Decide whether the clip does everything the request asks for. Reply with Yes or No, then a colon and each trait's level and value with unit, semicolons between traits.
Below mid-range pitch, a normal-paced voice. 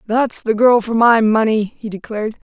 No: high, 220 Hz; average, 190 wpm